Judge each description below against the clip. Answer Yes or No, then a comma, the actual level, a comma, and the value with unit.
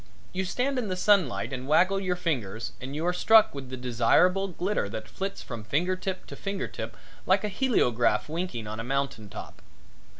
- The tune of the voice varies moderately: No, wide, 7.7 semitones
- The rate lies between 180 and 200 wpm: Yes, average, 195 wpm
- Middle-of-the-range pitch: Yes, medium, 165 Hz